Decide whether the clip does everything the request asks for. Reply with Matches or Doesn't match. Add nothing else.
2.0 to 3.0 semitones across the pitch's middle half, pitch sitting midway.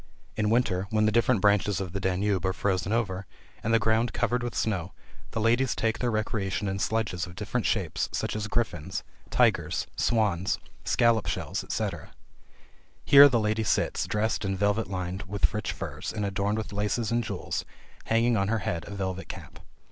Doesn't match